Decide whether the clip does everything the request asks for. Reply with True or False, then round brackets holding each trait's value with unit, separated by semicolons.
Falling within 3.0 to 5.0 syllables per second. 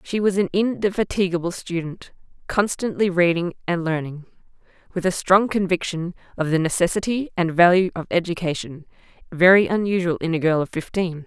False (5.4 syllables/s)